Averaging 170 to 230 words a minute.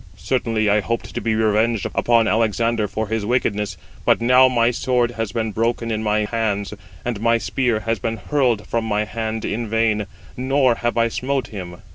Yes: average, 185 wpm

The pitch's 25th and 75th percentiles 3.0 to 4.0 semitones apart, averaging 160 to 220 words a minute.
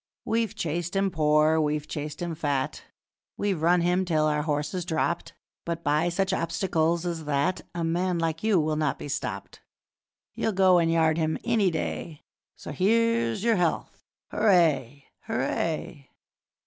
No: average, 3.3 semitones; average, 150 wpm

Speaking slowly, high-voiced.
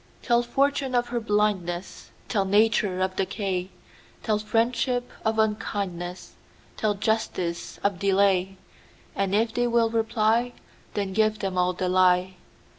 Yes: slow, 110 wpm; high, 205 Hz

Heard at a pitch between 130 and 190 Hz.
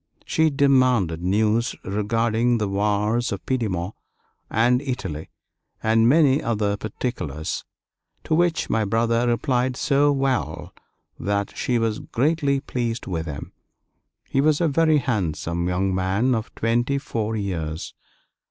No: low, 115 Hz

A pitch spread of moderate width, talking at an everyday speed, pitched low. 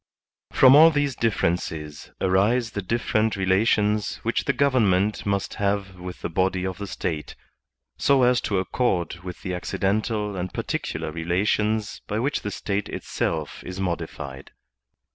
Yes: average, 3.3 semitones; average, 145 wpm; low, 100 Hz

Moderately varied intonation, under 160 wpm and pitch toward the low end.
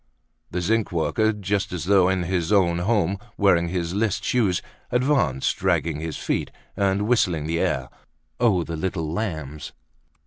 Yes: average, 3.6 semitones; average, 150 wpm; very low, 95 Hz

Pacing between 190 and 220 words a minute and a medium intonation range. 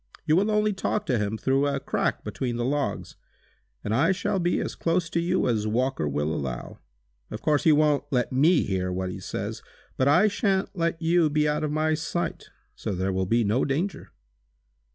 No: average, 200 wpm; wide, 6.9 semitones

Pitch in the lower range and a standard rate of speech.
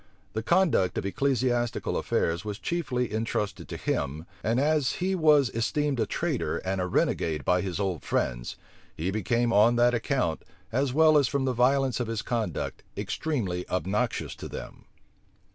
Yes: low, 120 Hz; average, 160 wpm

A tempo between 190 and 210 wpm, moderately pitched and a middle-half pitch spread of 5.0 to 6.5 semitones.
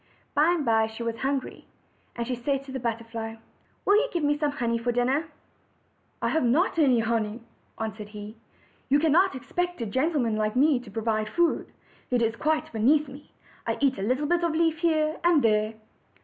No: average, 200 wpm; very high, 260 Hz; average, 5.3 semitones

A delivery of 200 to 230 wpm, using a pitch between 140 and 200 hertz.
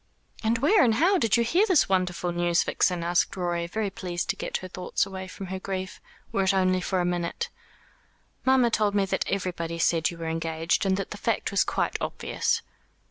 Yes: fast, 205 wpm; medium, 185 Hz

